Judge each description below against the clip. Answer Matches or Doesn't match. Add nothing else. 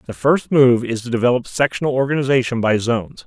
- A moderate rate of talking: Matches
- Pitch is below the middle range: Matches